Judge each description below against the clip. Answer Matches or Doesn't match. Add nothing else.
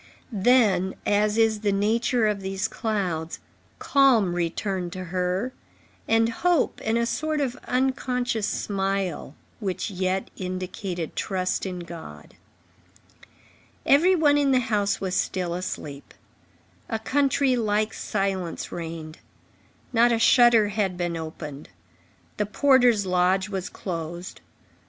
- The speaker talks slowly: Matches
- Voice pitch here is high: Matches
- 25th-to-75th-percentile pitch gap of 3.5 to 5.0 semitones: Matches